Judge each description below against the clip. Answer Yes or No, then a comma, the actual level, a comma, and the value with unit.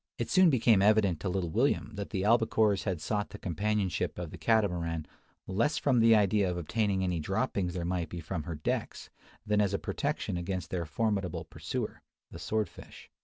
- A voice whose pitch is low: Yes, low, 100 Hz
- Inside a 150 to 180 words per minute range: No, average, 190 wpm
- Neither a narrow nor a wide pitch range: Yes, average, 3.7 semitones